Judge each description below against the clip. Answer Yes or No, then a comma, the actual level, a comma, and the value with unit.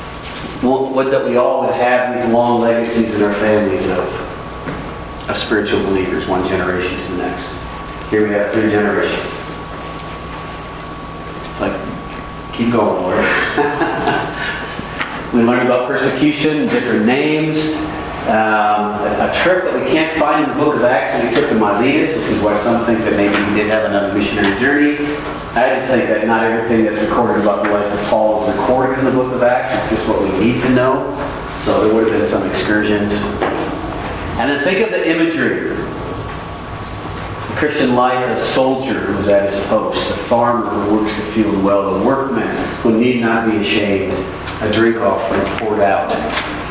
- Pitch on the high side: No, low, 110 Hz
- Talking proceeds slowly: No, average, 175 wpm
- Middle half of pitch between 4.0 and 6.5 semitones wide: No, average, 3.5 semitones